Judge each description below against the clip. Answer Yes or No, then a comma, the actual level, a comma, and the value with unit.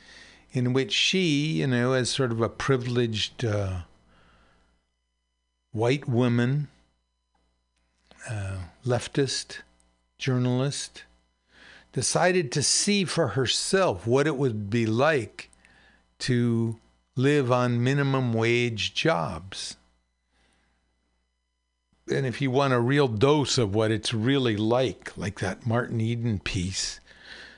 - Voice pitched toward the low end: Yes, low, 115 Hz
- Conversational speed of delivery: No, slow, 105 wpm